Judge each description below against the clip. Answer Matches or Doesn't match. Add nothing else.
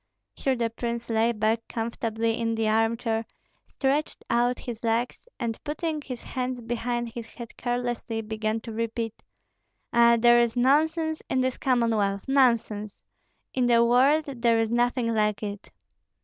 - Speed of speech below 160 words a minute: Matches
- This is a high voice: Matches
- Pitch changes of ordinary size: Doesn't match